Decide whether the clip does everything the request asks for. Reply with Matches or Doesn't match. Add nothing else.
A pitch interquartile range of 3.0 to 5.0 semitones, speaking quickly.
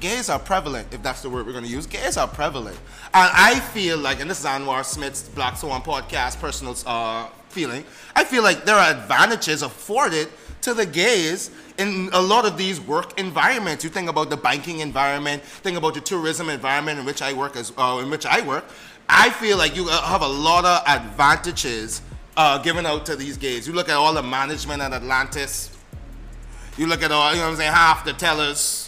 Matches